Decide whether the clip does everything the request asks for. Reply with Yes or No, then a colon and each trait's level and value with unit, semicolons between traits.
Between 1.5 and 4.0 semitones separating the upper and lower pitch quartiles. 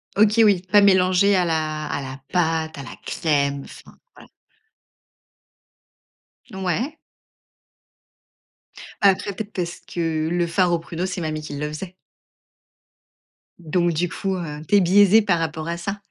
Yes: average, 3.5 semitones